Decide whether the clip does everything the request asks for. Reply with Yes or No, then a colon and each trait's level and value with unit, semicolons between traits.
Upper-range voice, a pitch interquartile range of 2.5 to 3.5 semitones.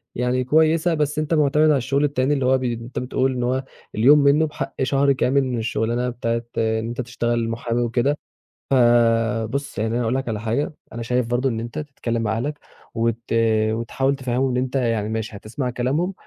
No: low, 125 Hz; average, 3.1 semitones